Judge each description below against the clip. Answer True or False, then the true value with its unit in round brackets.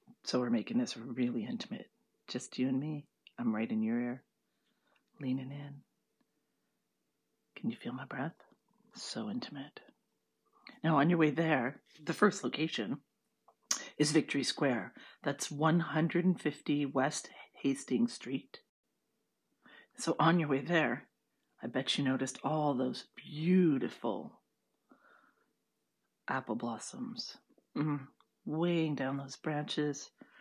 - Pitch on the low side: False (155 Hz)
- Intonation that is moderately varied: True (4.3 semitones)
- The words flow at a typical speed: False (115 wpm)